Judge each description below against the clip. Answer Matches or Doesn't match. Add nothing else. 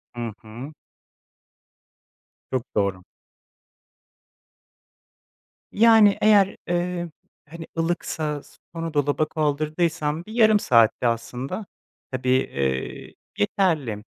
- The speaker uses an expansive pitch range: Matches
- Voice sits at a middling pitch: Matches